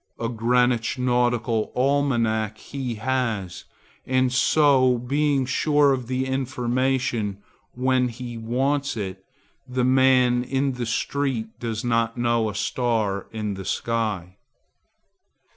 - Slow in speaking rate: Yes, slow, 115 wpm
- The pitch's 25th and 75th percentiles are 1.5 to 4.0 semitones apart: Yes, narrow, 2.5 semitones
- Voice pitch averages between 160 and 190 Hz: No, low, 125 Hz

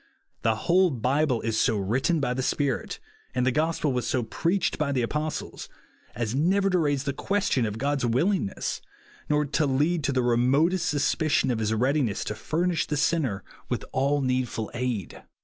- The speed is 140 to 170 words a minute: No, average, 185 wpm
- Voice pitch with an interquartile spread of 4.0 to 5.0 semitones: Yes, average, 4.3 semitones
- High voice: No, low, 135 Hz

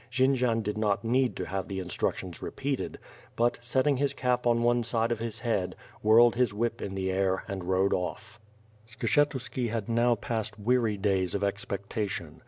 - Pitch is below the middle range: Yes, low, 115 Hz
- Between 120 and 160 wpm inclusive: No, average, 175 wpm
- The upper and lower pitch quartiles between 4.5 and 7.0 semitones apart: No, average, 3.4 semitones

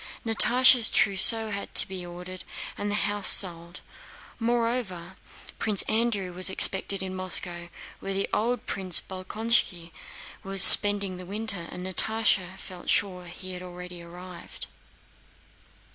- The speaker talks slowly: Yes, slow, 125 wpm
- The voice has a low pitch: No, high, 190 Hz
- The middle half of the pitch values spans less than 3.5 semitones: Yes, average, 2.9 semitones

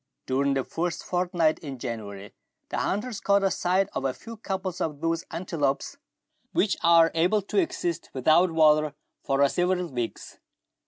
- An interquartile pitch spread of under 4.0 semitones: No, average, 4.8 semitones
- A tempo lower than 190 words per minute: Yes, average, 150 wpm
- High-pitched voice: No, medium, 165 Hz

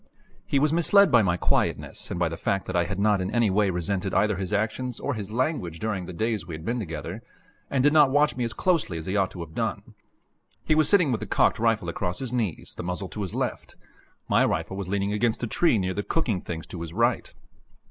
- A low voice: Yes, low, 105 Hz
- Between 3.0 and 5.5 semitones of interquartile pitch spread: Yes, average, 5.2 semitones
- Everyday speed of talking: No, fast, 245 wpm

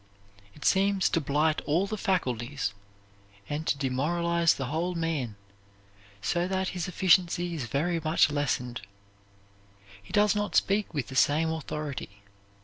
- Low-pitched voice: No, medium, 160 Hz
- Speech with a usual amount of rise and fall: Yes, average, 4.1 semitones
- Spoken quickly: No, average, 140 wpm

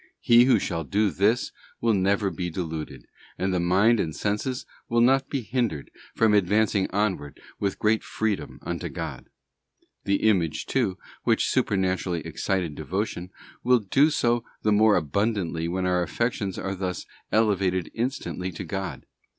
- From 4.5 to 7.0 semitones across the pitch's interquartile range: No, average, 3.6 semitones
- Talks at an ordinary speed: Yes, average, 150 wpm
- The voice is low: Yes, low, 100 Hz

